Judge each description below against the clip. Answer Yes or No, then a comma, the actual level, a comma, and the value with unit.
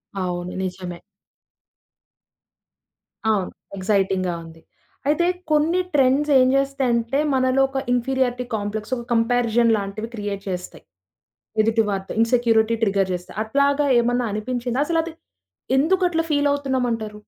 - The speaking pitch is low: No, high, 235 Hz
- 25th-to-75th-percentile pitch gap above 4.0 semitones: Yes, average, 4.8 semitones